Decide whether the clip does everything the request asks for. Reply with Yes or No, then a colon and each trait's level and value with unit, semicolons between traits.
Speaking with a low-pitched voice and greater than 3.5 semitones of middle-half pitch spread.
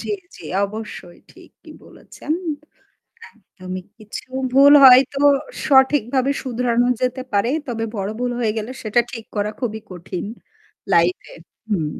No: high, 225 Hz; average, 3.9 semitones